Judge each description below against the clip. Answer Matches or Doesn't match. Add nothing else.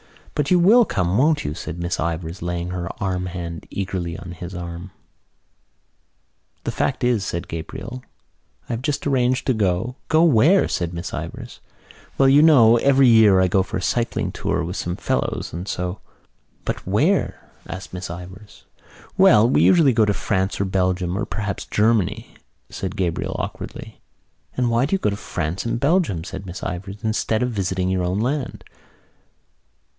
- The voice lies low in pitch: Matches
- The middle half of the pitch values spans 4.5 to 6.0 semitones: Matches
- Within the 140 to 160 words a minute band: Doesn't match